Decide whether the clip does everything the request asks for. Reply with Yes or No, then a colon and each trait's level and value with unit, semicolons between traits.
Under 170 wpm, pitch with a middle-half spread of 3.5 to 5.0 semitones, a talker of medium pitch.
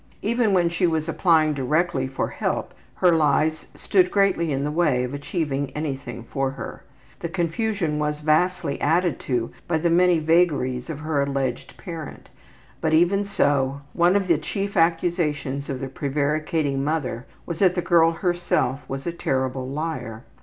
Yes: average, 160 wpm; average, 3.9 semitones; medium, 155 Hz